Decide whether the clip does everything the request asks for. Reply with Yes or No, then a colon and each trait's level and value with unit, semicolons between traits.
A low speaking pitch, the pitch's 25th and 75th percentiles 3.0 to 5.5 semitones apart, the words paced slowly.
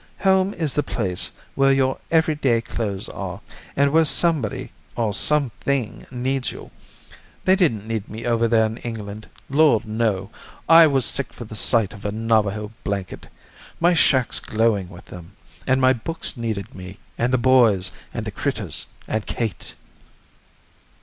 No: low, 115 Hz; average, 4.6 semitones; average, 155 wpm